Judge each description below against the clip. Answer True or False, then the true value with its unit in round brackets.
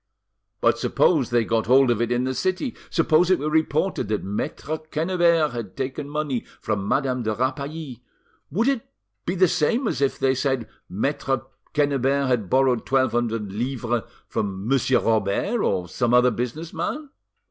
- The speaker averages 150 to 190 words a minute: True (165 wpm)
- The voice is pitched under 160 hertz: True (135 Hz)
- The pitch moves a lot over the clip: False (4.6 semitones)